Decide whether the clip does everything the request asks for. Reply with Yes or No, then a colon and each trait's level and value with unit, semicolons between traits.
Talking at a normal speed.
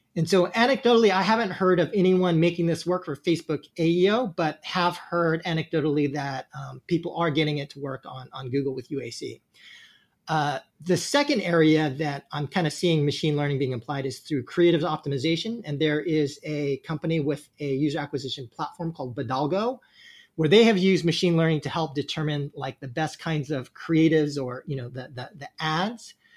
Yes: average, 185 wpm